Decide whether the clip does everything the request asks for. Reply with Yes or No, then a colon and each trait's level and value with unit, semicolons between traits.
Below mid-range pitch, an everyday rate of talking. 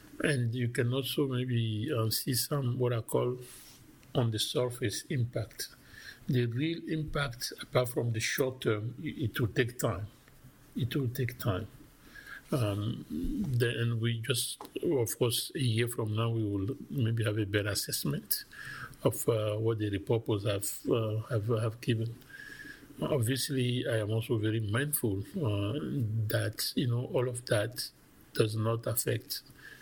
Yes: low, 120 Hz; average, 150 wpm